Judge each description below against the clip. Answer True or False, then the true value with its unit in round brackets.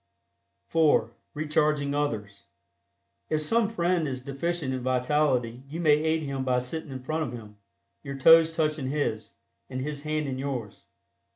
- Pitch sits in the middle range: True (145 Hz)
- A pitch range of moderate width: True (3.3 semitones)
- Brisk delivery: False (155 wpm)